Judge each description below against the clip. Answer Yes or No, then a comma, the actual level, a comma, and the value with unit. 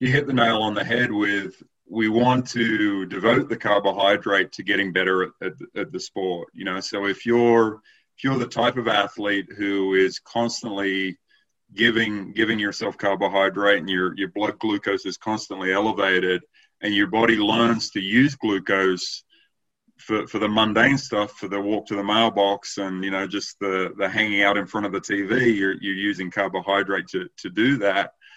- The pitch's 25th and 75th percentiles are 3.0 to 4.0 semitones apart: No, narrow, 2.5 semitones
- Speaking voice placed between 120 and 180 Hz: No, low, 100 Hz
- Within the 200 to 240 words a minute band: No, average, 185 wpm